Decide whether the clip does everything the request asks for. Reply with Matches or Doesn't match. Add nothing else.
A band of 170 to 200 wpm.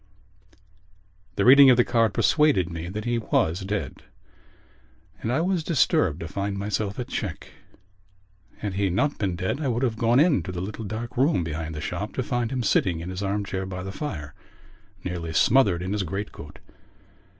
Matches